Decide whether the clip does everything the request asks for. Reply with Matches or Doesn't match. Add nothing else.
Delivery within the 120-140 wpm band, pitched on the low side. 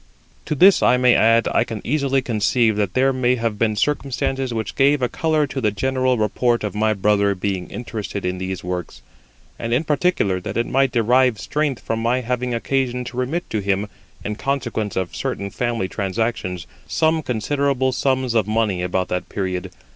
Doesn't match